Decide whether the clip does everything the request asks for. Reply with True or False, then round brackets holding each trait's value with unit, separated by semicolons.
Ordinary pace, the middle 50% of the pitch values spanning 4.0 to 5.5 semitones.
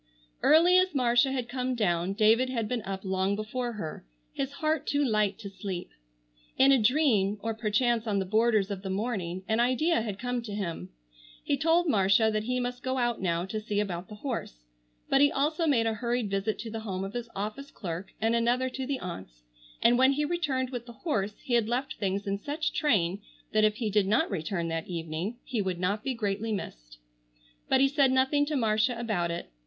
False (210 wpm; 4.7 semitones)